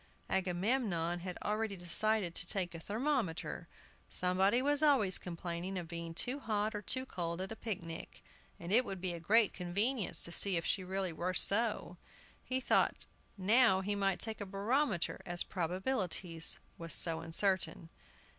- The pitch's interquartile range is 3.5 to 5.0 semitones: Yes, average, 3.9 semitones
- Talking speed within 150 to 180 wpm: Yes, average, 160 wpm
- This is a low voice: No, high, 190 Hz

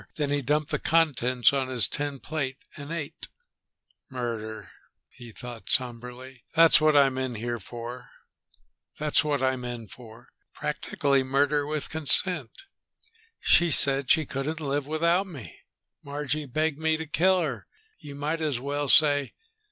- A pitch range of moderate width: Yes, average, 3.2 semitones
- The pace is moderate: No, slow, 130 wpm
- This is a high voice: No, medium, 140 Hz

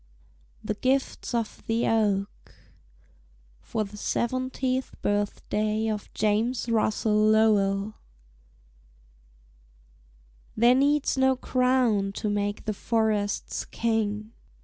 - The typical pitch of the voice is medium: No, high, 220 Hz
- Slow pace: Yes, slow, 90 wpm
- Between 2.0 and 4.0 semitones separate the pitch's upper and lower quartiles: Yes, average, 2.8 semitones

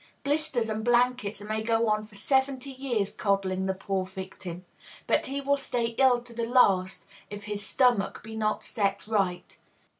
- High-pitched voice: Yes, high, 220 Hz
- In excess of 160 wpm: Yes, average, 170 wpm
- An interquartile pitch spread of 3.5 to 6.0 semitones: Yes, average, 3.9 semitones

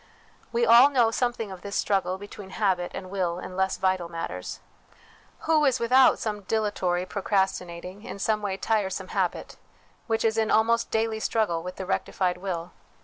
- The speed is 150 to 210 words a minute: Yes, average, 170 wpm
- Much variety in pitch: No, average, 3.5 semitones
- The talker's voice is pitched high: Yes, high, 200 Hz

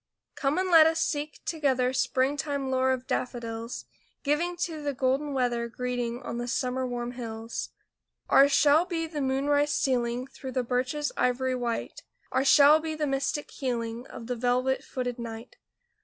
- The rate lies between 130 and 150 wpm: No, average, 160 wpm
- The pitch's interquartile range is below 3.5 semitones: Yes, average, 3.0 semitones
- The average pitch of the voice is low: No, very high, 260 Hz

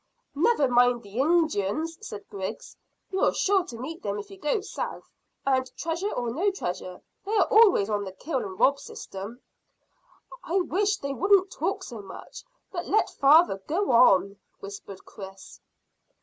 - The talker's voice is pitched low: No, very high, 275 Hz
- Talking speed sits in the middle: Yes, average, 160 wpm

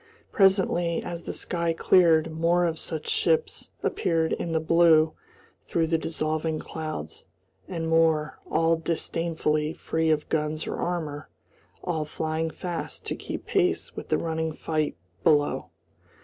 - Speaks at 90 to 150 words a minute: Yes, slow, 135 wpm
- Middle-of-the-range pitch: Yes, medium, 160 Hz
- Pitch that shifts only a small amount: Yes, narrow, 1.3 semitones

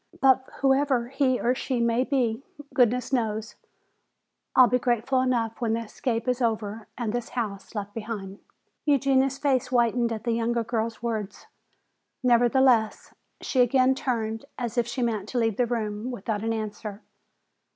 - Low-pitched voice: No, high, 235 Hz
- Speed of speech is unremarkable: Yes, average, 155 wpm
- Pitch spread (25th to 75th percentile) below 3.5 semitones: Yes, narrow, 2.4 semitones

